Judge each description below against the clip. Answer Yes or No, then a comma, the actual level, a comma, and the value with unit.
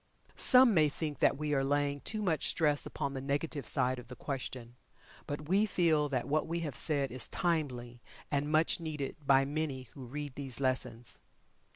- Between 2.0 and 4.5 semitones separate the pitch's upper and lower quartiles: Yes, average, 2.8 semitones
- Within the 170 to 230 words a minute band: Yes, average, 185 wpm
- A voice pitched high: No, medium, 145 Hz